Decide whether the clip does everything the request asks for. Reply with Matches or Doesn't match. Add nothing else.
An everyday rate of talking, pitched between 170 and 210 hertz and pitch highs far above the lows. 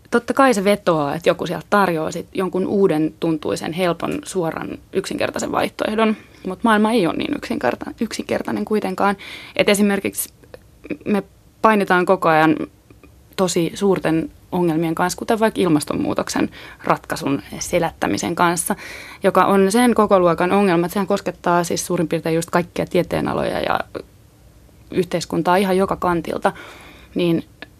Doesn't match